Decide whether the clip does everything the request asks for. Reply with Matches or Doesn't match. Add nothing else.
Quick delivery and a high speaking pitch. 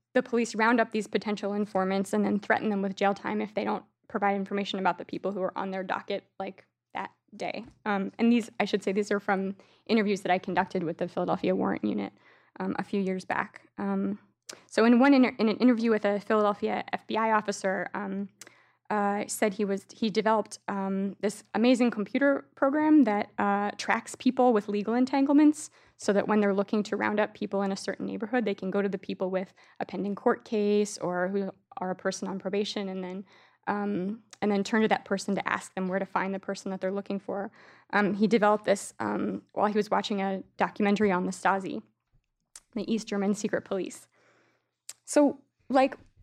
Matches